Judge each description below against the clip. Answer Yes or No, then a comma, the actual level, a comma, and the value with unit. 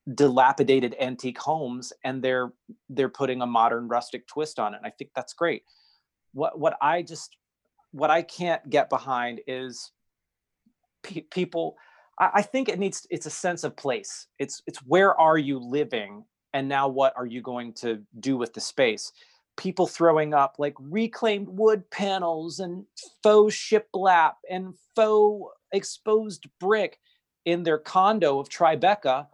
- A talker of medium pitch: Yes, medium, 160 Hz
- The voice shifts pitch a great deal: Yes, wide, 7.0 semitones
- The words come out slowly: No, average, 155 wpm